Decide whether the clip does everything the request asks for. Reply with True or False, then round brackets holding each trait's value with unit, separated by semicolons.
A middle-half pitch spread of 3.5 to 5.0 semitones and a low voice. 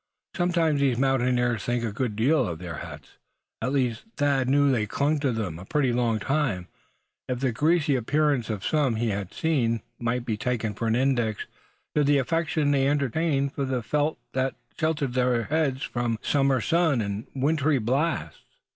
True (4.0 semitones; 130 Hz)